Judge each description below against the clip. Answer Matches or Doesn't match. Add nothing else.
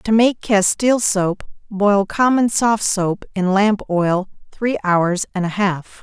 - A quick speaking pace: Doesn't match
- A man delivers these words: Doesn't match